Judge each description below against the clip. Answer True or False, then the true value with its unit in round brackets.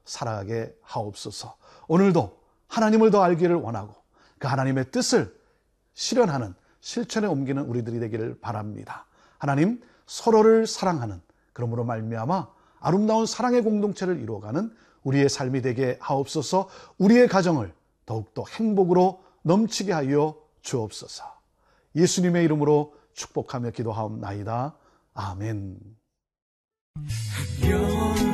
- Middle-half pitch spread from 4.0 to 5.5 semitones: False (8.8 semitones)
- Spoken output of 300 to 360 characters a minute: False (290 characters per minute)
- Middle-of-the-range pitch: True (145 Hz)